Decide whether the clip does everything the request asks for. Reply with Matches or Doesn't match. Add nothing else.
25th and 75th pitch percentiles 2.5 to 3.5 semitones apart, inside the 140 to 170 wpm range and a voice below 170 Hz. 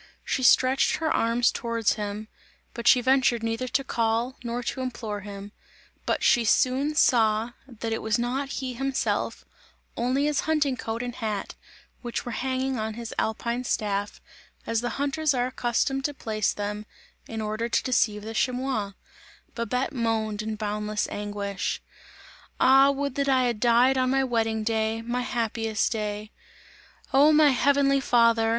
Doesn't match